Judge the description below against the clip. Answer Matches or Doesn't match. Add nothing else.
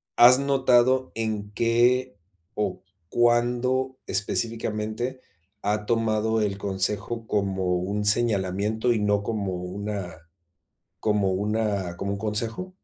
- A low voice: Matches